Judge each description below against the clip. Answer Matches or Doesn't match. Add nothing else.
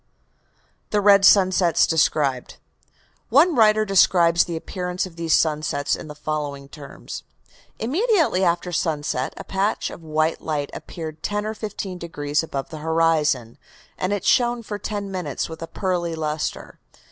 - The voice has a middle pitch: Matches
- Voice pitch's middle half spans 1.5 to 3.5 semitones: Doesn't match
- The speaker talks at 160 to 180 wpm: Doesn't match